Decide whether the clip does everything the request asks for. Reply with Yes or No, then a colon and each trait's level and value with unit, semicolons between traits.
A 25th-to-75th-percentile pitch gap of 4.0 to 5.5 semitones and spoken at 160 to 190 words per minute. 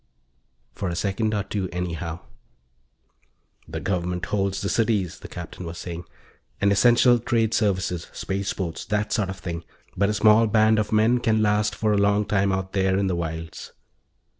No: average, 3.0 semitones; average, 170 wpm